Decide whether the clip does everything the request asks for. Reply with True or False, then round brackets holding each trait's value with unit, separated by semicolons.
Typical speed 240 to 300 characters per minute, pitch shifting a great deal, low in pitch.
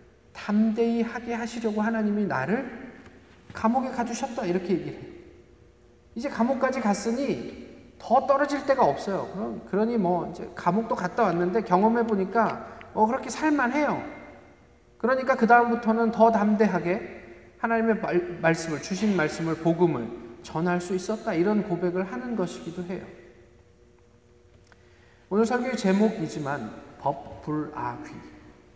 False (285 characters per minute; 5.9 semitones; 210 Hz)